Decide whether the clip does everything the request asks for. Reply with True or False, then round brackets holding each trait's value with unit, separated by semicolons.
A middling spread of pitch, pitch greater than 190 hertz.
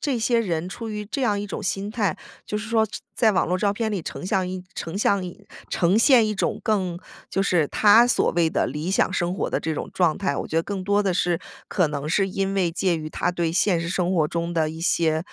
False (3.5 semitones; 185 Hz)